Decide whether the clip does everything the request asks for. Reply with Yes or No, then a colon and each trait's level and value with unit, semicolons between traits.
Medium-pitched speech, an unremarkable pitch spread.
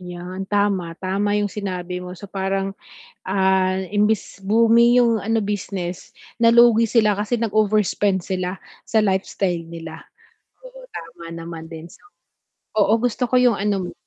No: high, 195 Hz; average, 3.1 semitones